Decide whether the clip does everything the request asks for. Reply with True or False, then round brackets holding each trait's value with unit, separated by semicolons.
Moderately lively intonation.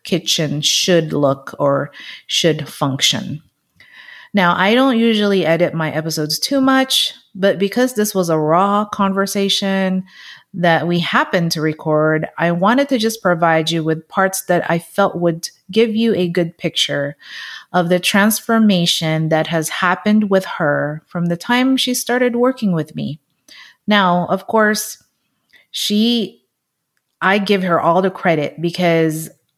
True (4.5 semitones)